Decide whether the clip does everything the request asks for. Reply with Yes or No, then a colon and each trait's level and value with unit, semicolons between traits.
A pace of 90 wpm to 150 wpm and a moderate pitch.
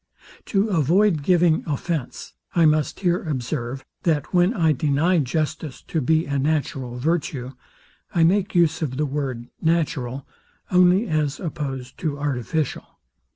Yes: slow, 135 wpm; medium, 155 Hz